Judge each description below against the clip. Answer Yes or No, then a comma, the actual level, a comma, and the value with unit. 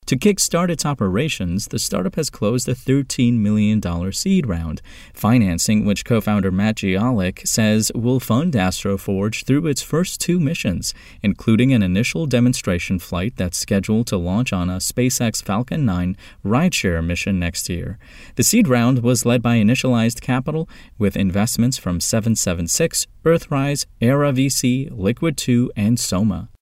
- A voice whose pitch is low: Yes, low, 115 Hz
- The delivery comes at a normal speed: Yes, average, 145 wpm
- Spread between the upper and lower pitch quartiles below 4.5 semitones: No, average, 4.9 semitones